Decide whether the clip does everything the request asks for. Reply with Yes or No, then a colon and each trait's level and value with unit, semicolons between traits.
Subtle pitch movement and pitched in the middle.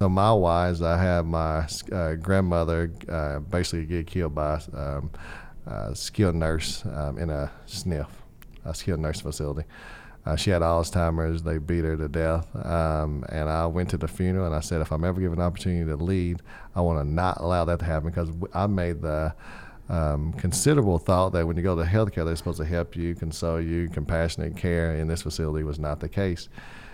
No: narrow, 2.1 semitones; very low, 85 Hz